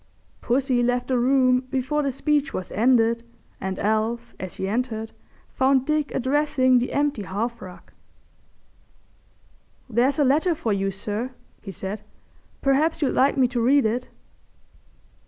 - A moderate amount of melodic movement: Yes, average, 3.5 semitones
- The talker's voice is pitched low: No, very high, 250 Hz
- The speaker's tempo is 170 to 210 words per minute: No, average, 140 wpm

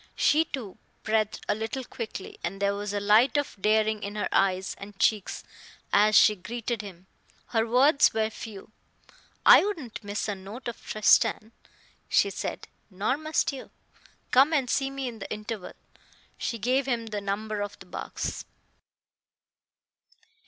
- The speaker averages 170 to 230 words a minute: No, average, 155 wpm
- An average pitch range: Yes, average, 3.5 semitones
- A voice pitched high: Yes, high, 220 Hz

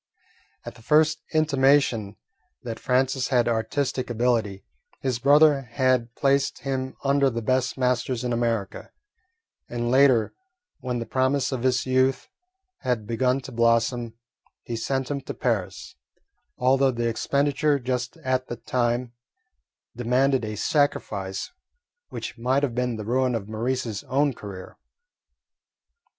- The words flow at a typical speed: No, slow, 130 wpm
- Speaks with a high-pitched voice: No, low, 125 Hz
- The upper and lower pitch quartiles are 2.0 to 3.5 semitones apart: Yes, narrow, 2.4 semitones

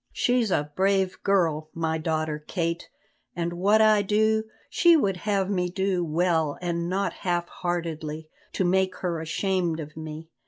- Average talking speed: Yes, average, 155 wpm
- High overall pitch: No, medium, 175 Hz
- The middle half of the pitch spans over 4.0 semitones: No, average, 3.2 semitones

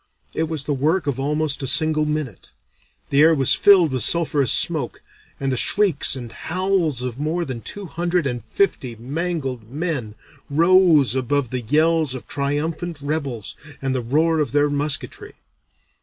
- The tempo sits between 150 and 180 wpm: Yes, average, 160 wpm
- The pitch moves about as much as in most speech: Yes, average, 3.8 semitones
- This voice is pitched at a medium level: Yes, medium, 145 Hz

